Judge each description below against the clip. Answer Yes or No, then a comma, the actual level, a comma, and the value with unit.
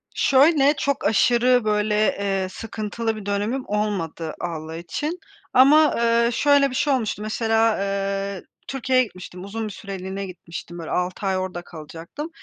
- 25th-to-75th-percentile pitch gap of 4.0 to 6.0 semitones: Yes, average, 4.8 semitones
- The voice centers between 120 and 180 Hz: No, high, 210 Hz